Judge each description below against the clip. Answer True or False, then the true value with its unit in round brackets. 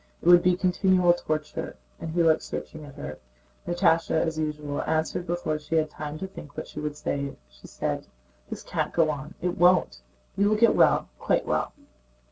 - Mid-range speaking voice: True (160 Hz)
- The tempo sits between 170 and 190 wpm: True (180 wpm)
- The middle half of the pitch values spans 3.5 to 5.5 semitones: False (2.8 semitones)